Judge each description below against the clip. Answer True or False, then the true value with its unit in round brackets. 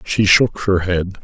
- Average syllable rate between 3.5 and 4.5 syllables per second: True (3.6 syllables/s)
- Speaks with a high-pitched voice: False (95 Hz)